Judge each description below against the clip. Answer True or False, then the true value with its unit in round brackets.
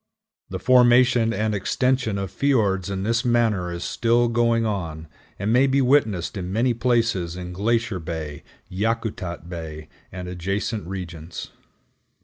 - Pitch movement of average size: True (4.8 semitones)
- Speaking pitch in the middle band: False (105 Hz)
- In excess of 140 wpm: False (135 wpm)